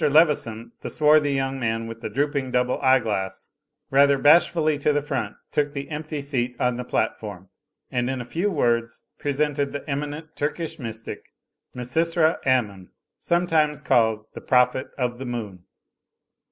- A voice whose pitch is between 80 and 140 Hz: Yes, low, 135 Hz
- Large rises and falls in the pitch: No, average, 3.9 semitones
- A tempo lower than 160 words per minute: Yes, average, 150 wpm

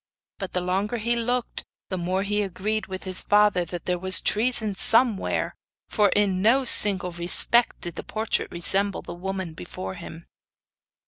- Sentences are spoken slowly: No, average, 165 wpm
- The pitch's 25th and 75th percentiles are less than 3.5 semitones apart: Yes, average, 3.0 semitones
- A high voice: Yes, high, 195 Hz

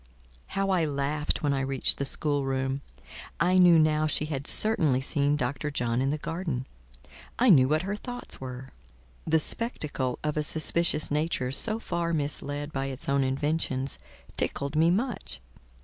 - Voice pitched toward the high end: No, medium, 150 Hz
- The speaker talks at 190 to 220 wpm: No, average, 160 wpm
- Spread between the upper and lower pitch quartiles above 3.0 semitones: Yes, average, 3.6 semitones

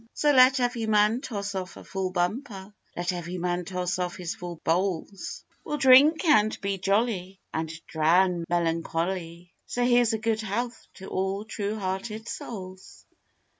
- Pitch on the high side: Yes, high, 195 Hz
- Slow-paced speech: No, average, 155 wpm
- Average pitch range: Yes, average, 4.0 semitones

